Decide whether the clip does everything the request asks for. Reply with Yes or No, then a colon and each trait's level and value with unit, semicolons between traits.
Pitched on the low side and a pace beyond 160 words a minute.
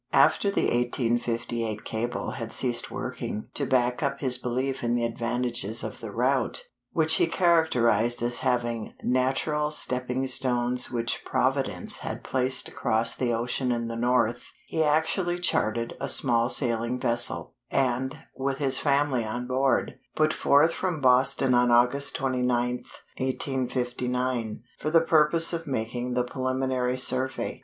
No: low, 125 Hz; average, 140 wpm